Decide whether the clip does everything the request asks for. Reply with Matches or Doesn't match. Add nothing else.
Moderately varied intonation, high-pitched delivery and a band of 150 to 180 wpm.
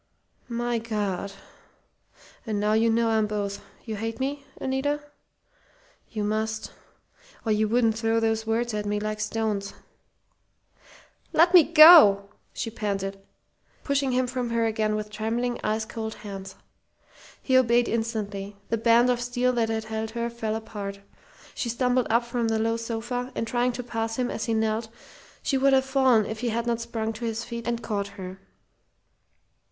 Doesn't match